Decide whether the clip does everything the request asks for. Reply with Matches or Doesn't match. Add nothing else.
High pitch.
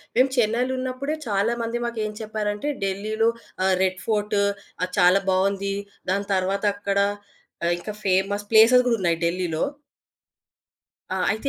Matches